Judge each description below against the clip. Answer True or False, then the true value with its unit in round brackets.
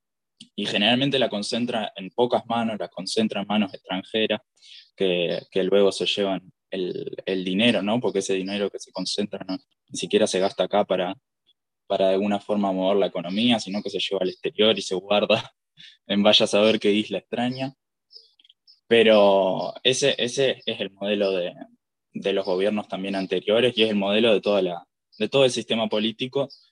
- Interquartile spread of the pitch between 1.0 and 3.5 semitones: True (2.7 semitones)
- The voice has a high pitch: False (105 Hz)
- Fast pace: False (180 wpm)